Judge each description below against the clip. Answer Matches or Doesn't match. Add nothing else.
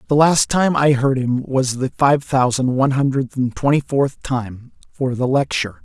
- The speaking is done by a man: Matches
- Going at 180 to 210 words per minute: Matches